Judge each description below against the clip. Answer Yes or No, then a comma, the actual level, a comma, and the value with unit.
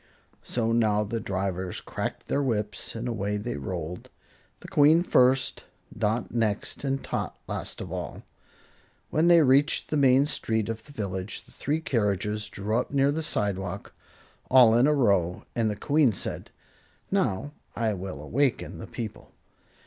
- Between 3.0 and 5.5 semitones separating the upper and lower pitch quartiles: Yes, average, 5.0 semitones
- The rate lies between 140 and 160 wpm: Yes, average, 155 wpm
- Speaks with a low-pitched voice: Yes, low, 115 Hz